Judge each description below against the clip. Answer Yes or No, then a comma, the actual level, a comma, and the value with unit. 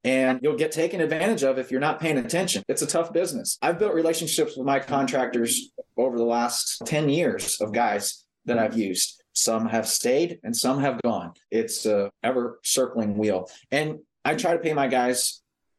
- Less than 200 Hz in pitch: Yes, medium, 140 Hz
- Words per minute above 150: Yes, average, 190 wpm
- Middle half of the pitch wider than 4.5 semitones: Yes, average, 4.9 semitones